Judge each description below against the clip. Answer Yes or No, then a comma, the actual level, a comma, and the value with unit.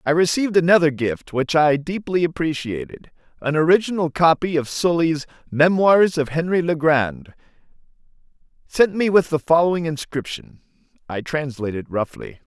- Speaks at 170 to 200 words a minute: No, slow, 135 wpm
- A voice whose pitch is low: No, medium, 160 Hz